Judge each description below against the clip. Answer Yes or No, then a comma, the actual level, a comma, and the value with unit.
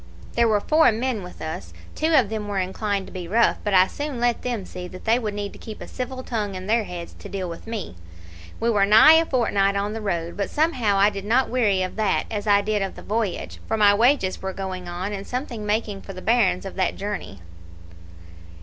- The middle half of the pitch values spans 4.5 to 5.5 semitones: No, average, 3.3 semitones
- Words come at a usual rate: No, fast, 235 wpm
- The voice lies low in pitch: No, high, 205 Hz